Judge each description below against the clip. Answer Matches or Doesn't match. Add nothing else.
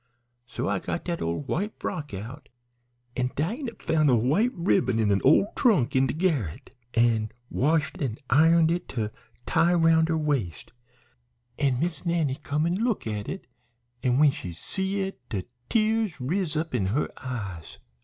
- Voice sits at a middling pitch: Matches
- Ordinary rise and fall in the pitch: Doesn't match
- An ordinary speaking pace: Matches